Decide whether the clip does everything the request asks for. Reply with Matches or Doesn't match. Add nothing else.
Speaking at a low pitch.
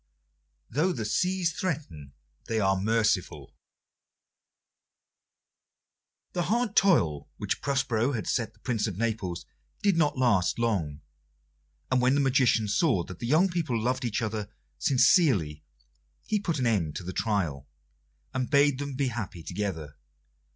Matches